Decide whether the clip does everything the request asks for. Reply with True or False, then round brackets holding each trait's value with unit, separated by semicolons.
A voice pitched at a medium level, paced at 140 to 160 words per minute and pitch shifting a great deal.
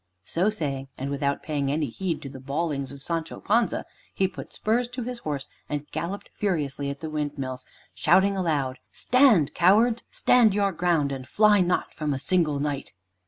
False (155 Hz; 175 wpm; 5.9 semitones)